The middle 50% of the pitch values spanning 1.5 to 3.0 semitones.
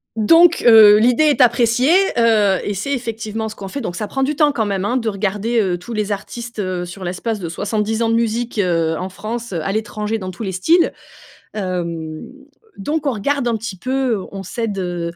No: average, 3.8 semitones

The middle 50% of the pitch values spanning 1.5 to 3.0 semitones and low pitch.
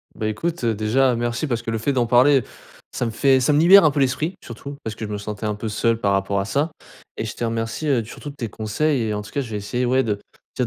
No: average, 4.1 semitones; low, 120 Hz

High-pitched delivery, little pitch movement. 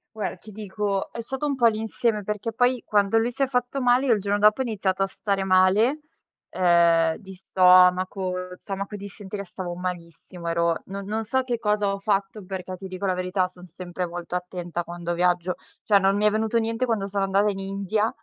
No: high, 195 Hz; average, 3.0 semitones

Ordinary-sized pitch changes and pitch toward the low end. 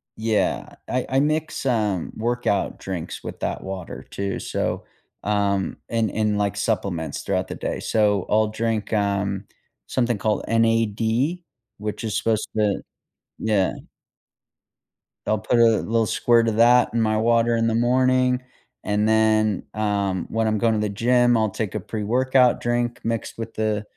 No: narrow, 2.2 semitones; low, 110 Hz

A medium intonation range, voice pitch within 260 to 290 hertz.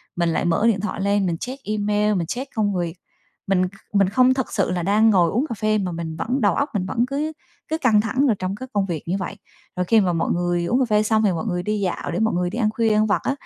No: average, 3.8 semitones; high, 205 Hz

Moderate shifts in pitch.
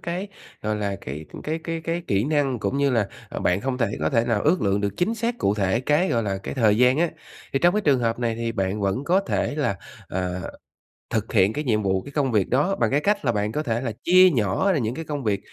No: wide, 6.9 semitones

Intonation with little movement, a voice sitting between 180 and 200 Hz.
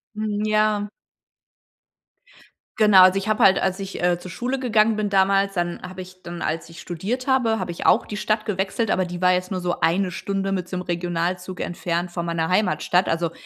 No: average, 3.1 semitones; medium, 185 Hz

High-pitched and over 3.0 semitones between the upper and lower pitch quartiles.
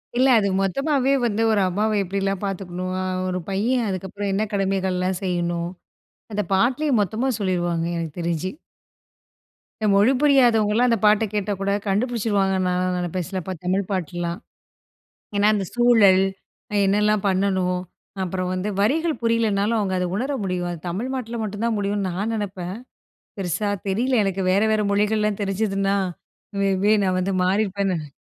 No: high, 200 Hz; average, 2.7 semitones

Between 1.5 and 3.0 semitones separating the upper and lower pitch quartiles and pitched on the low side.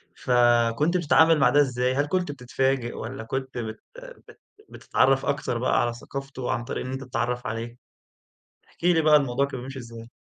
Yes: average, 2.7 semitones; low, 130 Hz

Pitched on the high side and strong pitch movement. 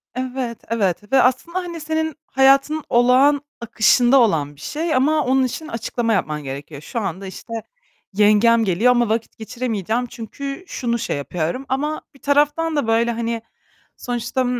No: high, 240 Hz; average, 3.9 semitones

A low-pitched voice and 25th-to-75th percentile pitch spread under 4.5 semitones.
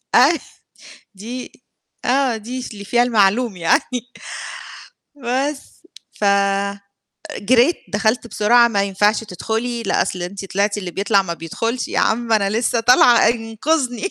No: high, 225 Hz; average, 3.4 semitones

